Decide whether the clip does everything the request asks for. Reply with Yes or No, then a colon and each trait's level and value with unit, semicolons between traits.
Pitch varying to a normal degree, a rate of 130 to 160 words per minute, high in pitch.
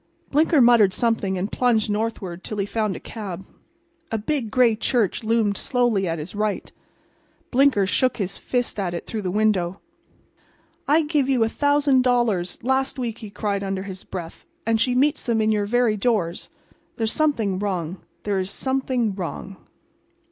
No: average, 4.1 semitones; average, 170 wpm; high, 220 Hz